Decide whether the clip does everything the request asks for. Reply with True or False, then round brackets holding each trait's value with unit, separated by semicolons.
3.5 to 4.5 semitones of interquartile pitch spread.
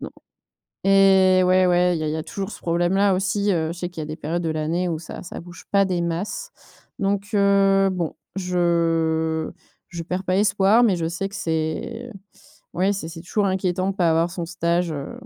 False (2.8 semitones)